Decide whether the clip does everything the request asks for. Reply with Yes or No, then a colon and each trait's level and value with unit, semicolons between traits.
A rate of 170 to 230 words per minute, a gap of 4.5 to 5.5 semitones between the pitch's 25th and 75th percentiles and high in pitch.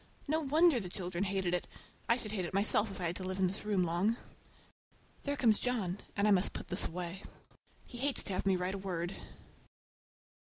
No: fast, 205 wpm; average, 3.6 semitones; high, 195 Hz